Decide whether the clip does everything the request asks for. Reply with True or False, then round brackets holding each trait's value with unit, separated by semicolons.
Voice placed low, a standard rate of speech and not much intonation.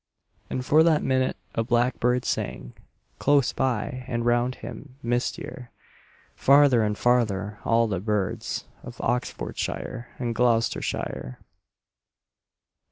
False (120 Hz; 105 wpm; 2.2 semitones)